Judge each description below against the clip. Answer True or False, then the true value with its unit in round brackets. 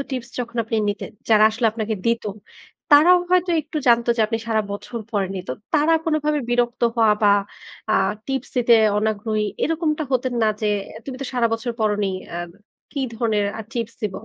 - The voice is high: True (230 Hz)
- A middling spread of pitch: True (3.7 semitones)